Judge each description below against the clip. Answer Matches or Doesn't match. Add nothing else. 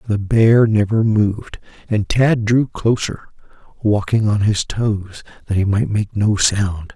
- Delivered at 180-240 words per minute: Doesn't match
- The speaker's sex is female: Doesn't match